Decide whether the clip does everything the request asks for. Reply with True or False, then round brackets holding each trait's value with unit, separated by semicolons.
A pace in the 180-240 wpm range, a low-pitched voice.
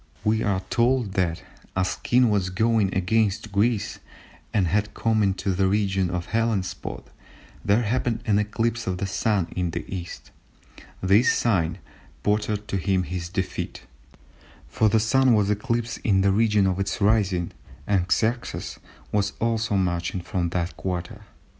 False (155 wpm; 100 Hz)